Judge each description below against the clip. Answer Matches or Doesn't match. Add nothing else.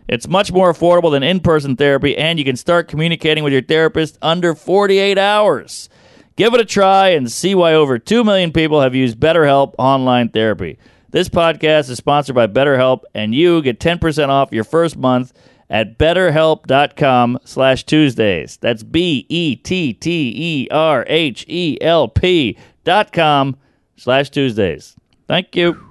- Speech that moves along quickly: Doesn't match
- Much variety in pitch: Doesn't match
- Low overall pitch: Doesn't match